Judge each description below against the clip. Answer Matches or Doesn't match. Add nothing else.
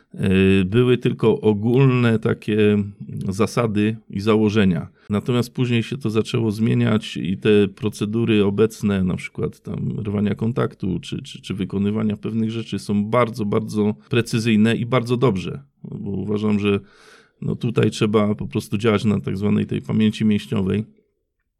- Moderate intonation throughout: Doesn't match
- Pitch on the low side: Matches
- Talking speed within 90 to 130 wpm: Doesn't match